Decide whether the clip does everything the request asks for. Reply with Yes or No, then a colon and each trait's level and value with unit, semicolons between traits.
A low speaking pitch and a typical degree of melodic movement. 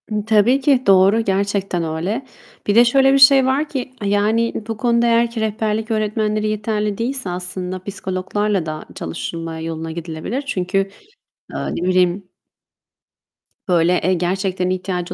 No: high, 205 Hz; average, 4.1 semitones